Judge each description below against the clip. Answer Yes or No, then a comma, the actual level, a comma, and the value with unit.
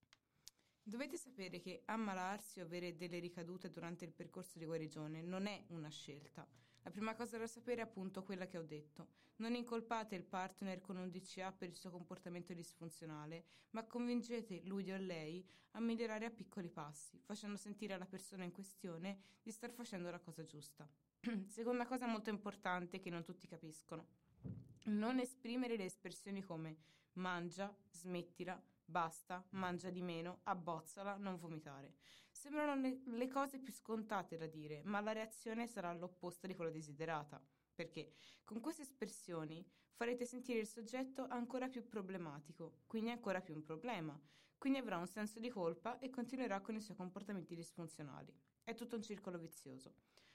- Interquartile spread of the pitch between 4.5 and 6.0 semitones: Yes, average, 4.8 semitones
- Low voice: No, medium, 185 Hz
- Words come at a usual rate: Yes, average, 160 wpm